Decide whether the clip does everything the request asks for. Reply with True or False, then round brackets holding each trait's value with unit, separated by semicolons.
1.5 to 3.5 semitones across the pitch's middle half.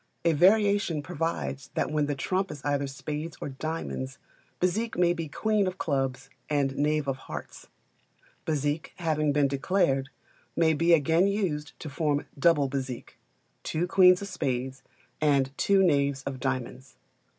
False (4.1 semitones)